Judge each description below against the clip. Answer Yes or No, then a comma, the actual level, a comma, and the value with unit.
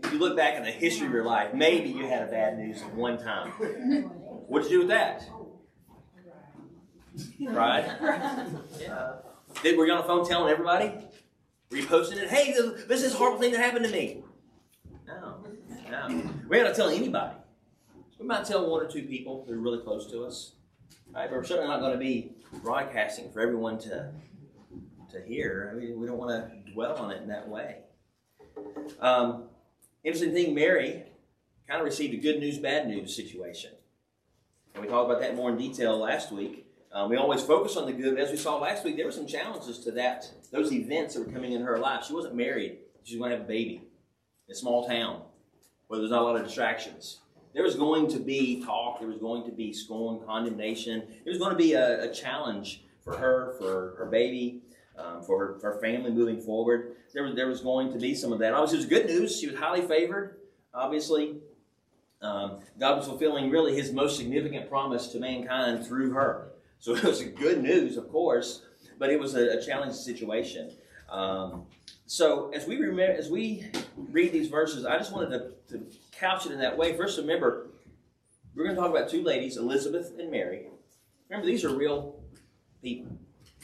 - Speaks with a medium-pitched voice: No, low, 130 Hz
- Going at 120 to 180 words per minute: No, average, 200 wpm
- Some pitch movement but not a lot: No, wide, 6.1 semitones